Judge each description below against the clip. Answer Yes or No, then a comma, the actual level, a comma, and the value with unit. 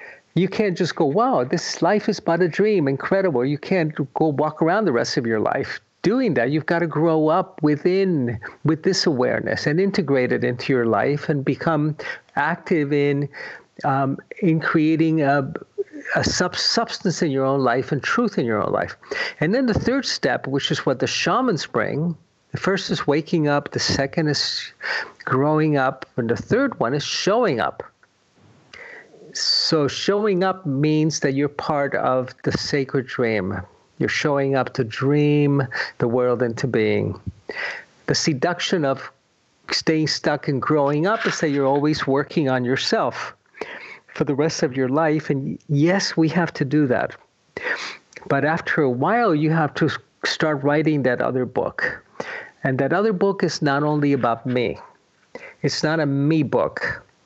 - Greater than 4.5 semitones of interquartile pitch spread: No, average, 3.7 semitones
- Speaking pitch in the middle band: Yes, medium, 150 Hz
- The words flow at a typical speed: Yes, average, 170 wpm